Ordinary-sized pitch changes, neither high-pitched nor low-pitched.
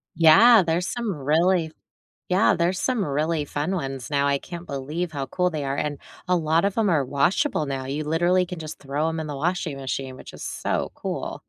Yes: average, 4.1 semitones; medium, 160 Hz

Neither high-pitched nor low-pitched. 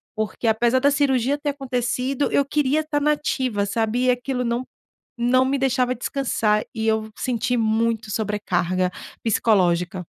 No: high, 245 Hz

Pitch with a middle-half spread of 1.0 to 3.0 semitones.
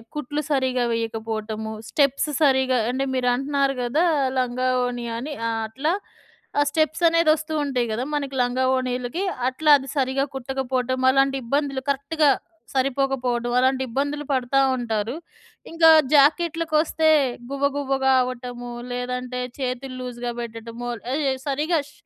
Yes: narrow, 2.5 semitones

